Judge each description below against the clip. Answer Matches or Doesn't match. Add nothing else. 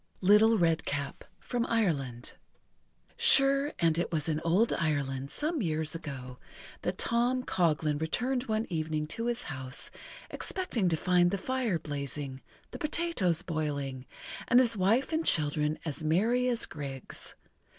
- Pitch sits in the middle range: Matches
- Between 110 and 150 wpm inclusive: Matches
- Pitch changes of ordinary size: Doesn't match